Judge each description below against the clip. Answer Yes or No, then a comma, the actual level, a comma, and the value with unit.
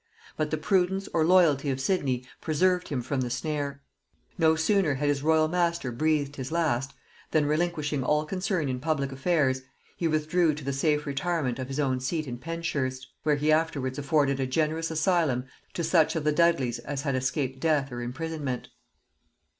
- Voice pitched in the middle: Yes, medium, 150 Hz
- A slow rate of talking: No, average, 180 wpm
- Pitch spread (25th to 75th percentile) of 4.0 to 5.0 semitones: No, average, 3.3 semitones